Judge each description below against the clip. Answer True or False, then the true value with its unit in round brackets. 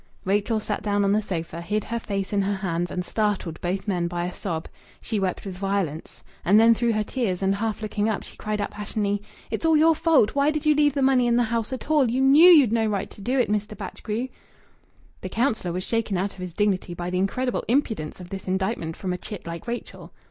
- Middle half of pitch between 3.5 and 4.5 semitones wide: True (3.9 semitones)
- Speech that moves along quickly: True (240 wpm)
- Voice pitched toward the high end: True (210 Hz)